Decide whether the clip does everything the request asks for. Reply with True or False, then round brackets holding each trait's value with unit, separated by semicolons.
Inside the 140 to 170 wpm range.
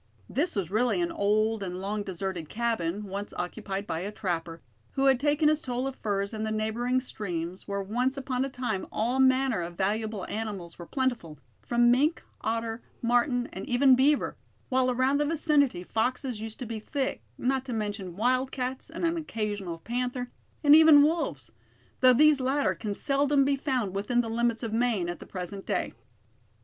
False (180 wpm)